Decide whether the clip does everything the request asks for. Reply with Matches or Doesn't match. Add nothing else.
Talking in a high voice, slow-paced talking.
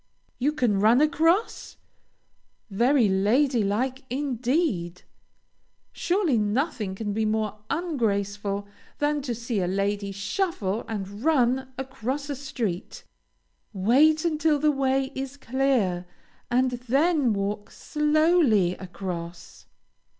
Matches